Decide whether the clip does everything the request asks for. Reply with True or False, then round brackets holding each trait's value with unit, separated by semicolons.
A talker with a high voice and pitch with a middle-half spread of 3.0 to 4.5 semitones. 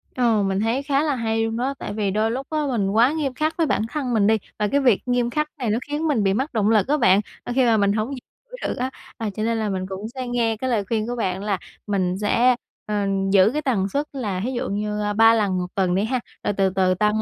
True (225 Hz; 3.9 semitones)